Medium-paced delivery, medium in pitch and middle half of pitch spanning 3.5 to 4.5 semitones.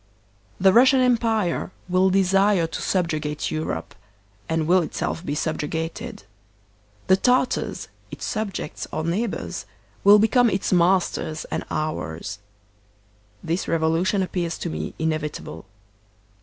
No: slow, 115 wpm; medium, 175 Hz; average, 3.8 semitones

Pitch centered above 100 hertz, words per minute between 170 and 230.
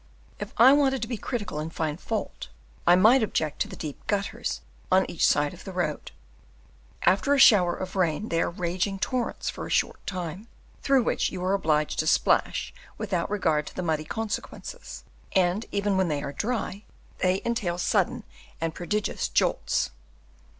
Yes: medium, 185 Hz; average, 175 wpm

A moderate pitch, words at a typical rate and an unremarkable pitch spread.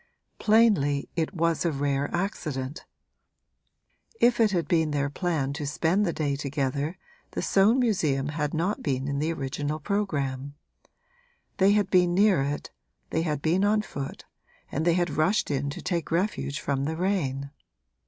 Yes: medium, 160 Hz; average, 160 wpm; average, 4.9 semitones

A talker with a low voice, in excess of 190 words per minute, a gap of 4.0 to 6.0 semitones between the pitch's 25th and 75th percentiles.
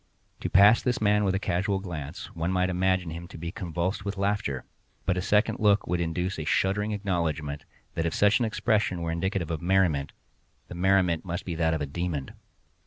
No: very low, 90 Hz; average, 200 wpm; average, 3.2 semitones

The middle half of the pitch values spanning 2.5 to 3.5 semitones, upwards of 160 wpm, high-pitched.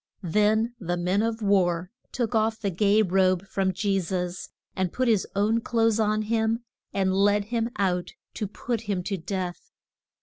Yes: average, 3.0 semitones; average, 170 wpm; high, 205 Hz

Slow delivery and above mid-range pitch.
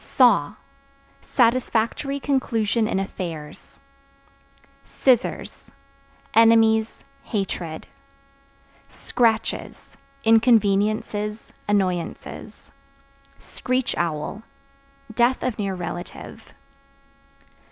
Yes: slow, 60 wpm; high, 220 Hz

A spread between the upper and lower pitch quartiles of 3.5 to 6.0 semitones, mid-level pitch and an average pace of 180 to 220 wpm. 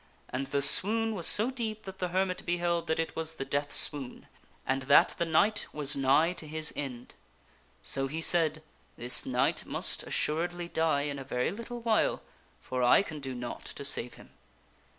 Yes: average, 4.8 semitones; medium, 155 Hz; average, 190 wpm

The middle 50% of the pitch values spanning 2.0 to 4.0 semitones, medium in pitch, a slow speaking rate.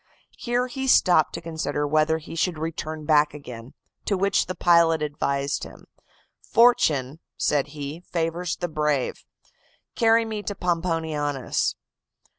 Yes: average, 3.4 semitones; medium, 160 Hz; slow, 130 wpm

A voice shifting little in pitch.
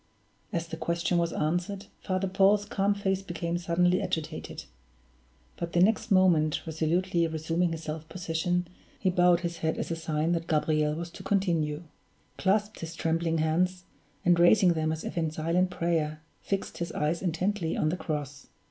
Yes: narrow, 2.3 semitones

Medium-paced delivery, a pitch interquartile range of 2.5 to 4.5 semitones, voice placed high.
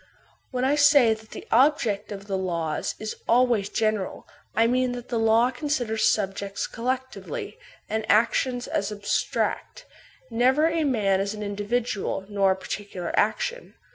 Yes: average, 150 wpm; average, 3.9 semitones; high, 225 Hz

